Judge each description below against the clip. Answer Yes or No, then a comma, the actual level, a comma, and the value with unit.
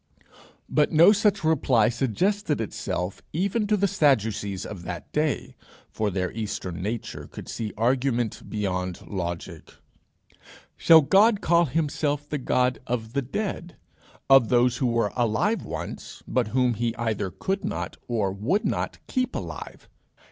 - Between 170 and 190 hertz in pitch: No, low, 125 Hz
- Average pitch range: No, wide, 7.3 semitones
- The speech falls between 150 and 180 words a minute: No, average, 140 wpm